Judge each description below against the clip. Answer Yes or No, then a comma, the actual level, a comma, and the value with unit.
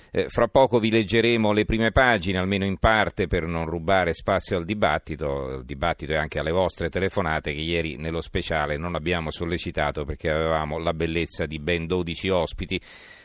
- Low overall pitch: Yes, very low, 85 Hz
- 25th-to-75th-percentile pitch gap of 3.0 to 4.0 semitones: Yes, average, 3.4 semitones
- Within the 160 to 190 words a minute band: Yes, fast, 170 wpm